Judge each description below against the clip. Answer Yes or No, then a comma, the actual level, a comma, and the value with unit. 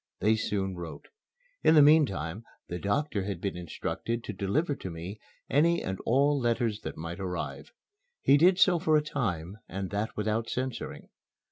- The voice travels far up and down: Yes, wide, 7.0 semitones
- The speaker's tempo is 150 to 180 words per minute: Yes, average, 165 wpm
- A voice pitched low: Yes, low, 110 Hz